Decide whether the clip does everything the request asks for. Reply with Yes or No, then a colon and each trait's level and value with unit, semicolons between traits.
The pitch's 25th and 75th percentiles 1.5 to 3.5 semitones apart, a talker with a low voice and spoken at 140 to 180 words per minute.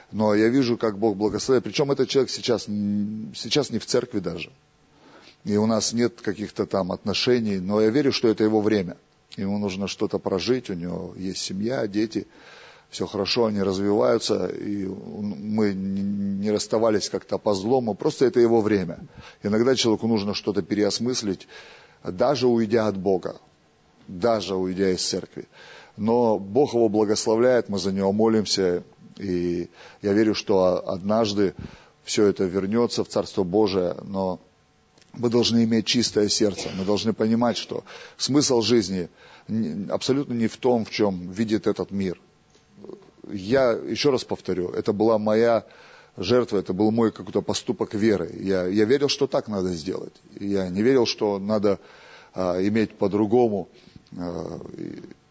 Yes: average, 2.9 semitones; low, 105 Hz; average, 150 wpm